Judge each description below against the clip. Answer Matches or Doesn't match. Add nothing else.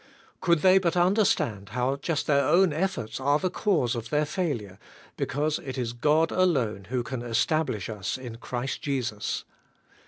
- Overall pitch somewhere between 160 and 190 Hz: Doesn't match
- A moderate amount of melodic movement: Doesn't match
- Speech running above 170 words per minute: Doesn't match